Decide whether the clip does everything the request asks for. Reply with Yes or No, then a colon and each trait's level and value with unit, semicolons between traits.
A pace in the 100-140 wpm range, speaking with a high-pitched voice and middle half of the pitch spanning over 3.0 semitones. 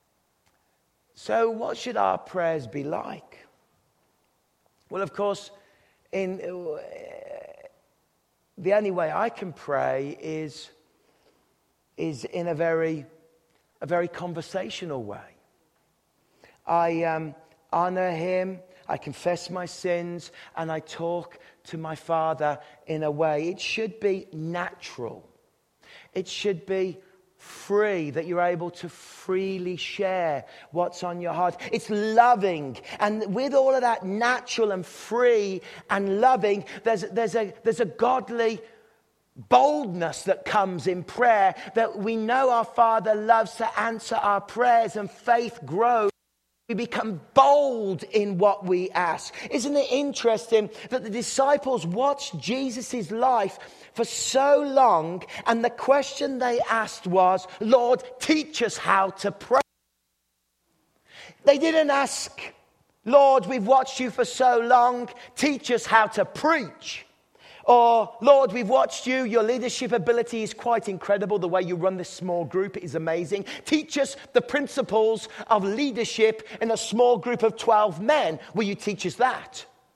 Yes: slow, 135 wpm; high, 210 Hz; average, 5.3 semitones